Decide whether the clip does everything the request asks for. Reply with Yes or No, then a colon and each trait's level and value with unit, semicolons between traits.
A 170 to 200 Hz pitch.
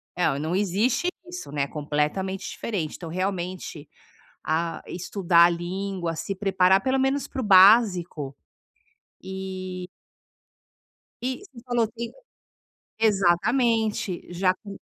Yes: high, 190 Hz